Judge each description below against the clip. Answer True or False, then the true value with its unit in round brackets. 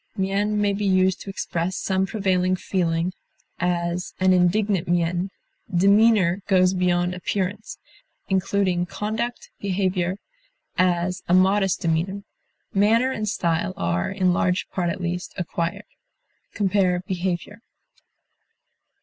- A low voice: False (185 Hz)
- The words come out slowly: True (115 wpm)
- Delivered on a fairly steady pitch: True (2.1 semitones)